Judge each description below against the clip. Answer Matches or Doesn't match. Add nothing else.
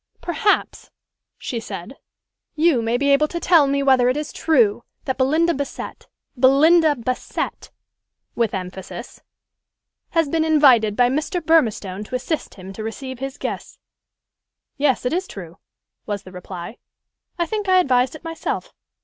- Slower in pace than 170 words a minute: Matches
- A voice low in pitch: Doesn't match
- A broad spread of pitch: Matches